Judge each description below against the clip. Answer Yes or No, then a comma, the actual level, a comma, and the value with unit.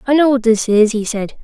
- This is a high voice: Yes, high, 235 Hz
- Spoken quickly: Yes, fast, 290 wpm